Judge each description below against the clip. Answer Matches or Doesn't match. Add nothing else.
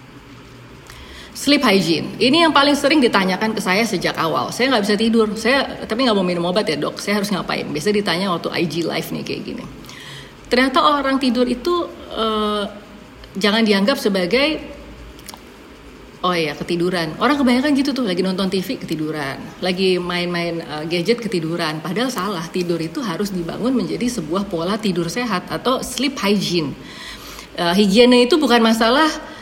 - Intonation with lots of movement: Matches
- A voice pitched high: Matches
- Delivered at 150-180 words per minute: Matches